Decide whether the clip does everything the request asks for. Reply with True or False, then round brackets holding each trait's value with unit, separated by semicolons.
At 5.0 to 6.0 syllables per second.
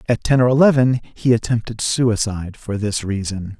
True (5.1 syllables/s)